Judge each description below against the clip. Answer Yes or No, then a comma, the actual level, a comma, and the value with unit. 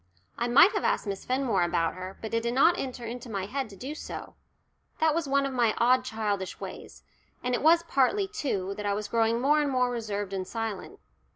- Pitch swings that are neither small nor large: Yes, average, 5.0 semitones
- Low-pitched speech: No, high, 240 Hz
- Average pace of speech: No, fast, 220 wpm